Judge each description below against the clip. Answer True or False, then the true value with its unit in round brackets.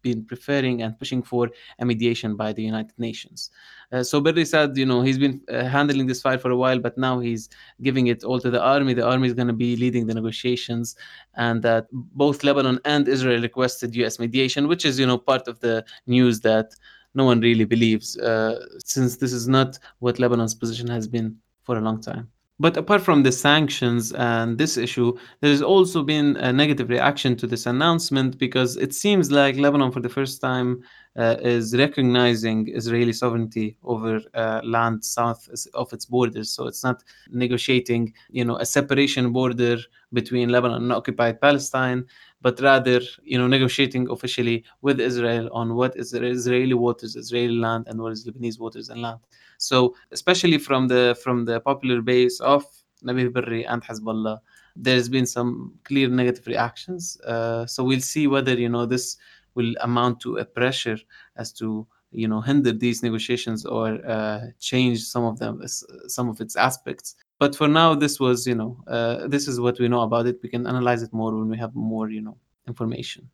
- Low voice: True (125 Hz)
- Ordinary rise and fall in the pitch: False (2.0 semitones)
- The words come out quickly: False (190 wpm)